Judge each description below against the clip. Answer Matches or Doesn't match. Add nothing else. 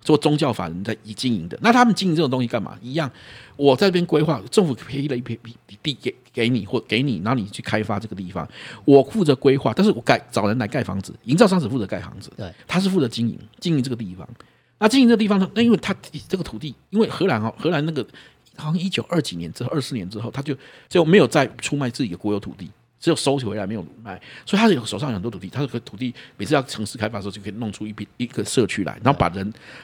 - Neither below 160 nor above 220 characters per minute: Doesn't match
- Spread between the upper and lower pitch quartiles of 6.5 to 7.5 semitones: Matches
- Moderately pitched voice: Doesn't match